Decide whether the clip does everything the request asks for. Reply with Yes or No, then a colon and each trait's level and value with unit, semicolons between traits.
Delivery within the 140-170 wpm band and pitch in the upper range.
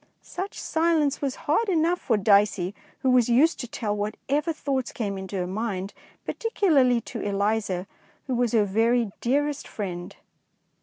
Yes: average, 160 wpm; high, 235 Hz